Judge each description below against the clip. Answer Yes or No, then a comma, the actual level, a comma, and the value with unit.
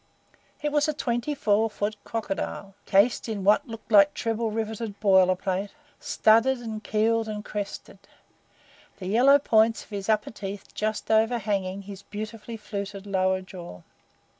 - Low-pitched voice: No, high, 215 Hz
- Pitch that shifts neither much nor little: No, narrow, 2.3 semitones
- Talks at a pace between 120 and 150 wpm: Yes, average, 145 wpm